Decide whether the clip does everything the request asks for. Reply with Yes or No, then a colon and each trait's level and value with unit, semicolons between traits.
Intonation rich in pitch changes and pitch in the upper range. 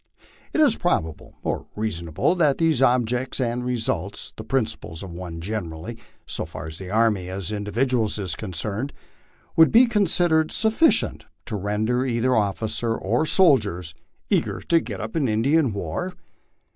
No: wide, 5.8 semitones; low, 115 Hz